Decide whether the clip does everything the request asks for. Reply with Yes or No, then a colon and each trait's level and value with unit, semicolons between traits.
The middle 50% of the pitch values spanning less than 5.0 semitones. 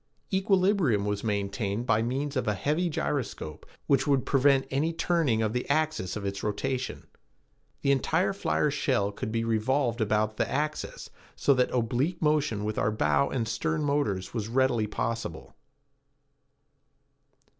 No: average, 5.3 semitones